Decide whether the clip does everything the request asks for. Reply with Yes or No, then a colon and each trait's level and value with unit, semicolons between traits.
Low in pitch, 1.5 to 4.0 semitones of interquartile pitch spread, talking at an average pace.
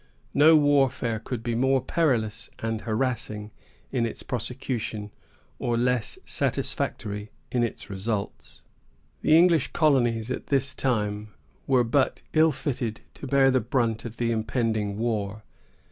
No: low, 120 Hz; average, 3.5 semitones; slow, 130 wpm